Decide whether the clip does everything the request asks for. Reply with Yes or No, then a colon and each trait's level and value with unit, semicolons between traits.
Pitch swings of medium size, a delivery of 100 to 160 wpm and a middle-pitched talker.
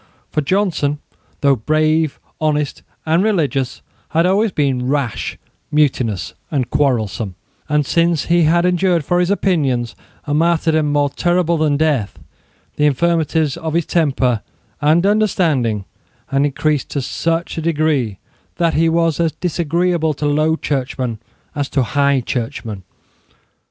Yes: average, 3.5 semitones; slow, 135 wpm; medium, 155 Hz